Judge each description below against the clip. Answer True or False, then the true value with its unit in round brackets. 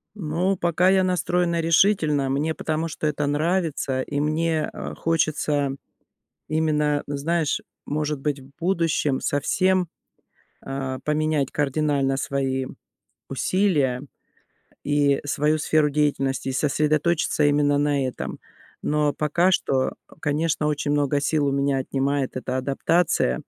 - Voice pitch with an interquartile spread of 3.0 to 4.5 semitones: False (2.5 semitones)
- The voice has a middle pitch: True (150 Hz)